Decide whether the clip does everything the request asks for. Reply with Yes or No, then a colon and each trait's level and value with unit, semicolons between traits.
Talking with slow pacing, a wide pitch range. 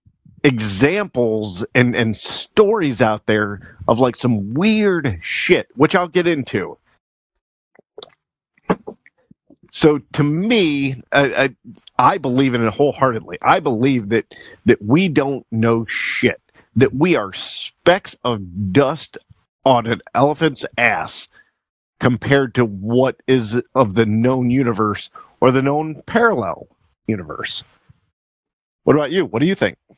No: slow, 125 wpm; average, 4.2 semitones